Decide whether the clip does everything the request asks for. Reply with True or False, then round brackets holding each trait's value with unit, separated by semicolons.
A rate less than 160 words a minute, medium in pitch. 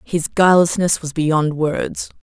True (135 wpm; 165 Hz)